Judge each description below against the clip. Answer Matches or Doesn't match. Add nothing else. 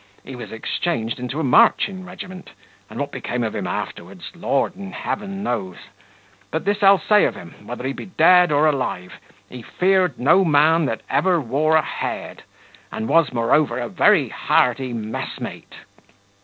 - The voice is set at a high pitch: Doesn't match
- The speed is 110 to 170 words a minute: Matches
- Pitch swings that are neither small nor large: Doesn't match